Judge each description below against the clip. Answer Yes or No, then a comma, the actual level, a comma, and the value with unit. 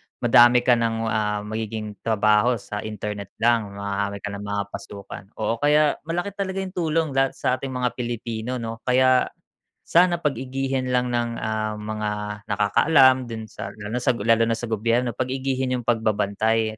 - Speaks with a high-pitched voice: No, low, 115 Hz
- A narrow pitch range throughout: No, average, 3.3 semitones